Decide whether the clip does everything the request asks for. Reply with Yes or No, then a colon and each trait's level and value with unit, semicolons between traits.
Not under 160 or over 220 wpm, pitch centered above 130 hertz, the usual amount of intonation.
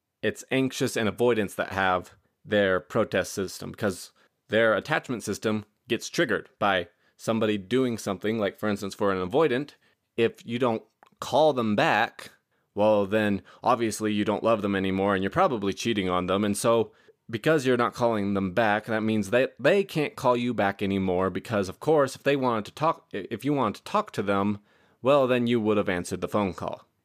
No: average, 195 wpm; low, 110 Hz; average, 3.3 semitones